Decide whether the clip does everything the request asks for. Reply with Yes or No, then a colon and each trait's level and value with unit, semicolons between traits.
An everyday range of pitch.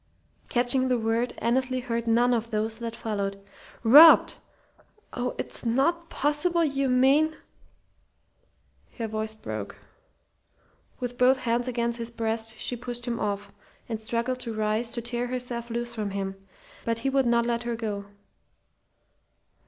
No: narrow, 2.0 semitones